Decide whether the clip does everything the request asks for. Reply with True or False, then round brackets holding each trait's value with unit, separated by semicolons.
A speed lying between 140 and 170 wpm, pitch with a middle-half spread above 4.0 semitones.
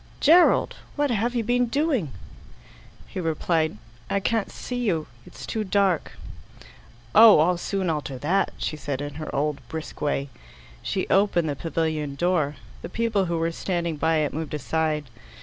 True (160 wpm; 5.0 semitones)